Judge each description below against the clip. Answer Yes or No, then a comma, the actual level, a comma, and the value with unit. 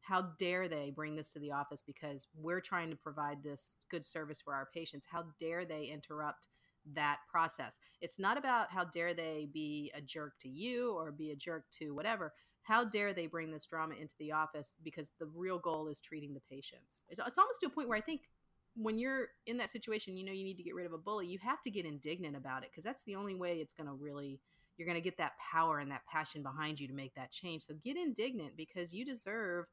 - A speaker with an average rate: No, fast, 240 wpm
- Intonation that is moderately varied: Yes, average, 4.0 semitones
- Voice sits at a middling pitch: Yes, medium, 160 Hz